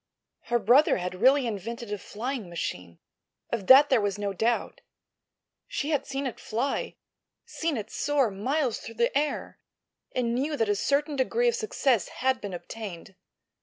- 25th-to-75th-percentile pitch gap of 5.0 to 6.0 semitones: Yes, average, 5.3 semitones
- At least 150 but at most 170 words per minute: Yes, average, 155 wpm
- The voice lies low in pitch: No, high, 240 Hz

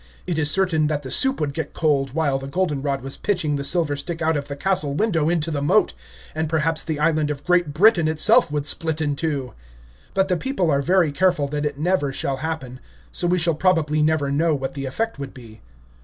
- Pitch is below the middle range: No, medium, 155 Hz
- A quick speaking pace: Yes, fast, 225 wpm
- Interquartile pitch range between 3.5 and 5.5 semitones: No, average, 3.0 semitones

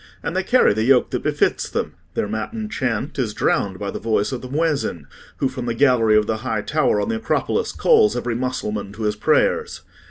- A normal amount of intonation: No, wide, 6.1 semitones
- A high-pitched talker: No, low, 125 Hz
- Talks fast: Yes, fast, 215 wpm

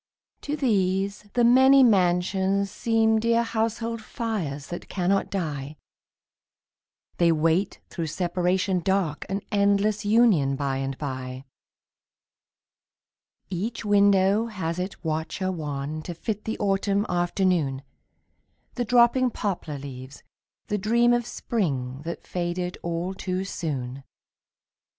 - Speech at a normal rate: No, slow, 115 wpm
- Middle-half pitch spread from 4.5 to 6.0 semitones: Yes, average, 5.0 semitones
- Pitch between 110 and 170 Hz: No, high, 190 Hz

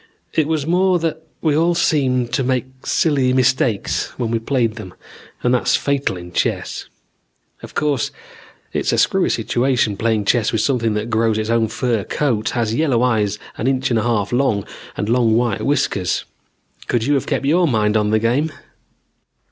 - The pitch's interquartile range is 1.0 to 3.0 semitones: No, average, 3.8 semitones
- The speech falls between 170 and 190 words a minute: Yes, average, 180 wpm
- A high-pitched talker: No, low, 120 Hz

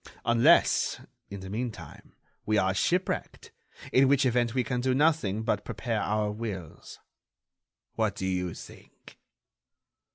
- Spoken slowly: Yes, slow, 130 wpm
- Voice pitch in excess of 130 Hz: No, low, 115 Hz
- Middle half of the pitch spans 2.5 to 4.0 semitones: No, average, 4.5 semitones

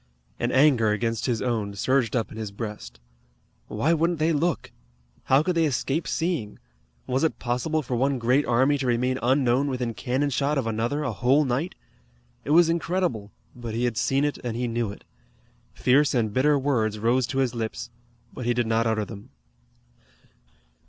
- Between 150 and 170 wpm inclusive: No, average, 180 wpm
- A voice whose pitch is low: Yes, low, 125 Hz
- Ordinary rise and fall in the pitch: Yes, average, 3.9 semitones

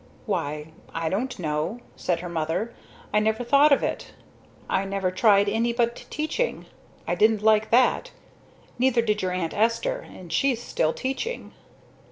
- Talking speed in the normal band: Yes, average, 155 wpm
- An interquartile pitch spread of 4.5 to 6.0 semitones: Yes, average, 5.2 semitones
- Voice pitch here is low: No, high, 215 Hz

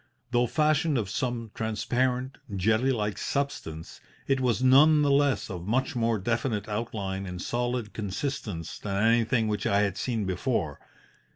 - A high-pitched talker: No, low, 115 Hz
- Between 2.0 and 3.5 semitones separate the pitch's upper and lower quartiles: No, average, 4.3 semitones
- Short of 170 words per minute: Yes, average, 150 wpm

